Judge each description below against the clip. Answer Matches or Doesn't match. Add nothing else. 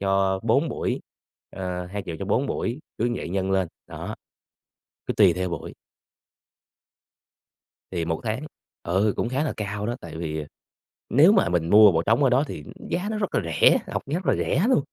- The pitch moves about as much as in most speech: Doesn't match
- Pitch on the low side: Matches